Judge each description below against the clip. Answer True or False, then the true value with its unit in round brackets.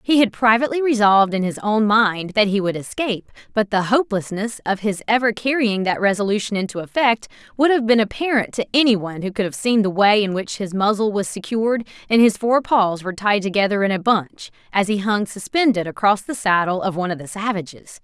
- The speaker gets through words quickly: True (215 wpm)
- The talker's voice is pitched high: True (210 Hz)